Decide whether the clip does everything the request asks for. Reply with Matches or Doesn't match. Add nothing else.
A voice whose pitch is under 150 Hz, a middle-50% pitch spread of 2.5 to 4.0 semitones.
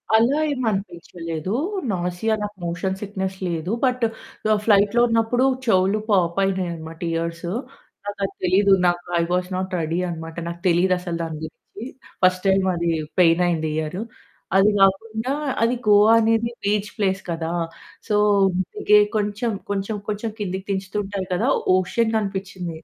Doesn't match